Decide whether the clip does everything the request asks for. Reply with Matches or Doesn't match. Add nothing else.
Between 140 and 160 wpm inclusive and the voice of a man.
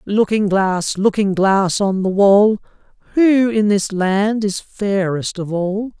Matches